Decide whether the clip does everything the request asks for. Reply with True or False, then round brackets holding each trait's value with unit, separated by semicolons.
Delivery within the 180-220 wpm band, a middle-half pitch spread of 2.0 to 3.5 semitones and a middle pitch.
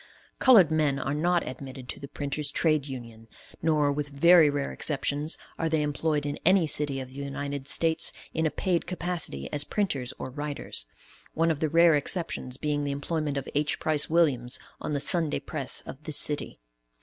True (185 wpm; 2.5 semitones; 150 Hz)